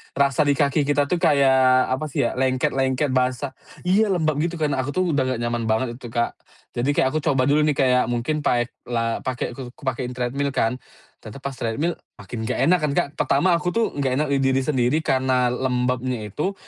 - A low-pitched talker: Yes, low, 130 Hz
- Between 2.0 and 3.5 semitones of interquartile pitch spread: Yes, average, 2.8 semitones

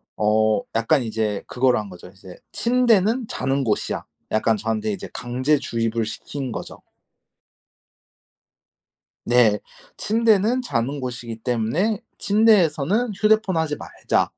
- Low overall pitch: Yes, low, 130 Hz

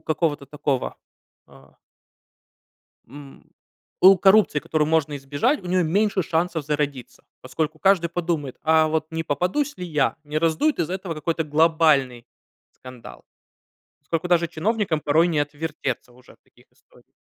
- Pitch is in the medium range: Yes, medium, 160 Hz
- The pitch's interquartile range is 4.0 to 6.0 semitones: No, average, 3.1 semitones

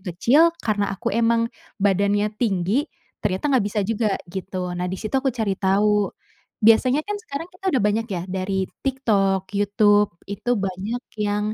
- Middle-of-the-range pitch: No, high, 210 Hz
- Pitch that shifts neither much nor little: Yes, average, 3.0 semitones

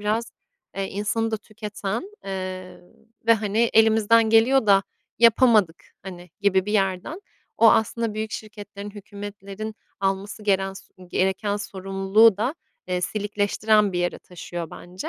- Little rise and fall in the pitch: Yes, narrow, 2.3 semitones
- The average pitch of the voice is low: No, high, 205 Hz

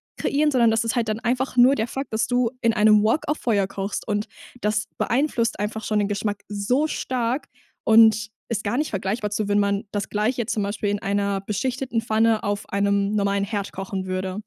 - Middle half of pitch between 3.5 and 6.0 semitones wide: No, average, 2.7 semitones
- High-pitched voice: Yes, high, 215 Hz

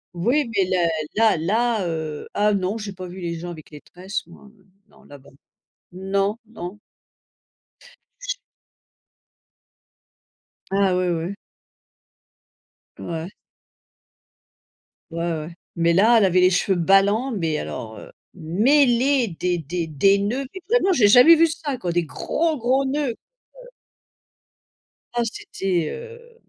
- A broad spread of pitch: Yes, wide, 5.8 semitones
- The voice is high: Yes, high, 195 Hz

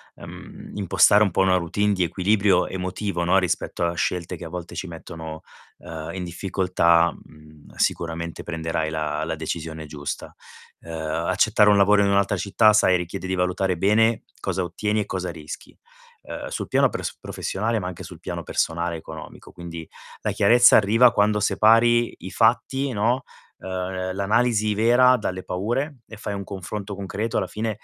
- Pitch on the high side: No, very low, 95 Hz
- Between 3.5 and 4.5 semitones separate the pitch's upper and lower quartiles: Yes, average, 3.8 semitones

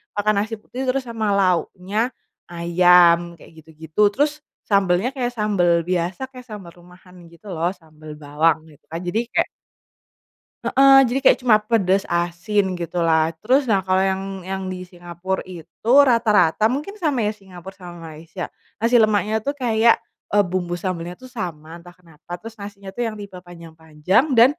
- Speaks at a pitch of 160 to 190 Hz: Yes, medium, 185 Hz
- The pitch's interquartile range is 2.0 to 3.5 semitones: No, average, 4.1 semitones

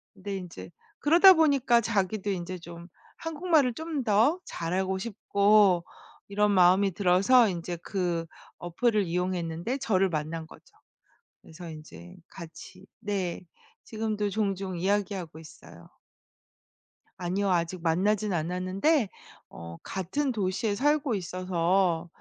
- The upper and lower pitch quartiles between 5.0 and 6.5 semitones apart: No, average, 3.6 semitones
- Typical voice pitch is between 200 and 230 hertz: No, high, 190 Hz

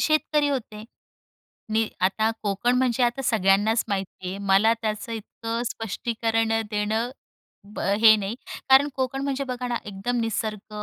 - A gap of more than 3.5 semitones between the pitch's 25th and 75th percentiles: No, average, 2.8 semitones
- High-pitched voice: Yes, high, 225 Hz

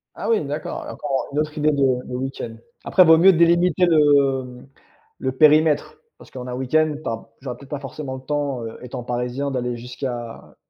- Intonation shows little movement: No, average, 3.5 semitones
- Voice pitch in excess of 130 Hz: Yes, medium, 140 Hz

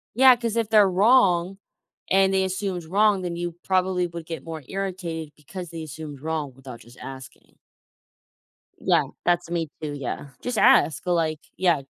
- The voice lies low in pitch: No, medium, 175 Hz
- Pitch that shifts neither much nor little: Yes, average, 3.4 semitones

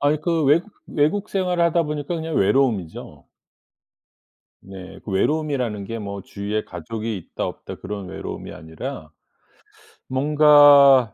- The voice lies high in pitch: No, low, 135 Hz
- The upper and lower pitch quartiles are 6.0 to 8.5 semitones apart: Yes, wide, 7.2 semitones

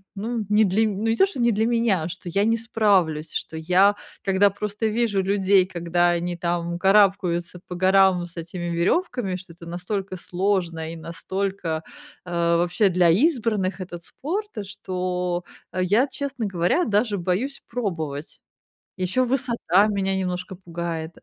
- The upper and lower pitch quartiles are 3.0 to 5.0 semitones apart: Yes, average, 3.4 semitones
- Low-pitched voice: No, high, 190 Hz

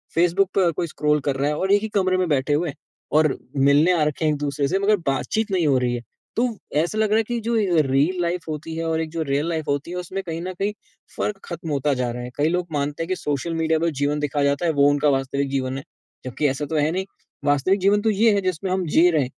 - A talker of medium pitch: Yes, medium, 160 Hz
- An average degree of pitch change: Yes, average, 4.4 semitones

